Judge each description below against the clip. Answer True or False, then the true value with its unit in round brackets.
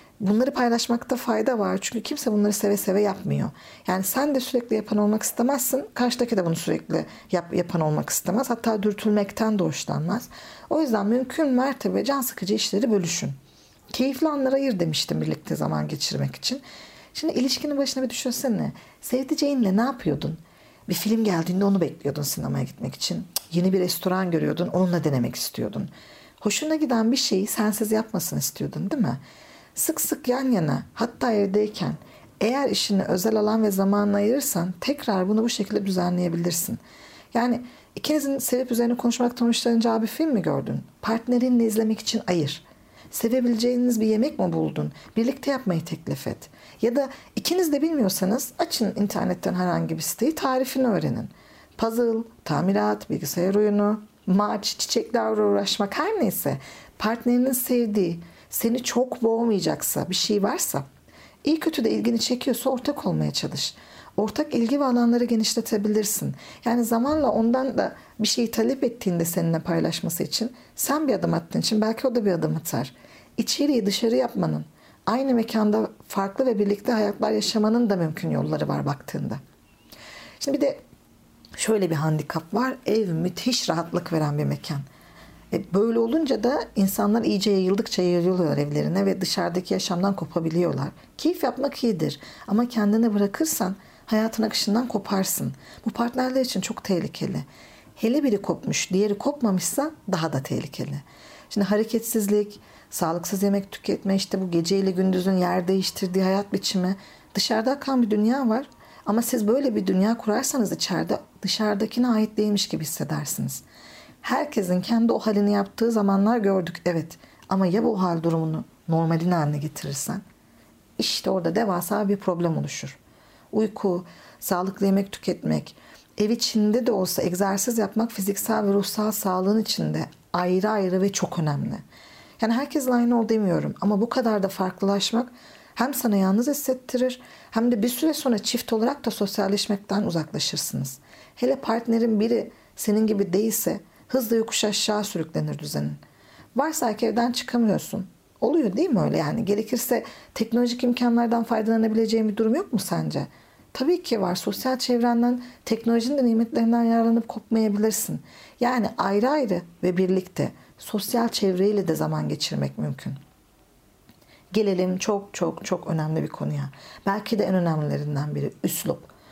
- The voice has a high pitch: True (215 Hz)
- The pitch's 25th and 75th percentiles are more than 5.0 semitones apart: False (4.3 semitones)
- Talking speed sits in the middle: False (145 wpm)